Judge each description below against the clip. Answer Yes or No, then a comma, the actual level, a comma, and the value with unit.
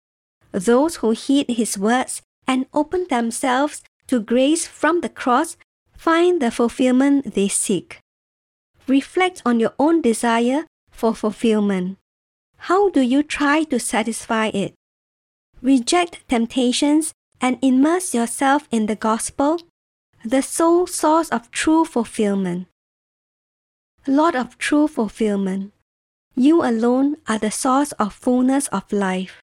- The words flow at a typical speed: No, slow, 120 wpm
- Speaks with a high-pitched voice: Yes, very high, 255 Hz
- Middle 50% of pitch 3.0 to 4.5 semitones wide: No, average, 5.1 semitones